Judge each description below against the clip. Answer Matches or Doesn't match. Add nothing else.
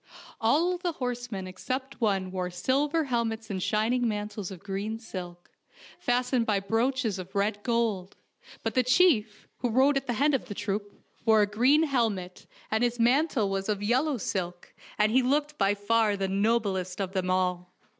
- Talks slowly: Doesn't match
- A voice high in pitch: Matches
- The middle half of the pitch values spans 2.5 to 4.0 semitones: Doesn't match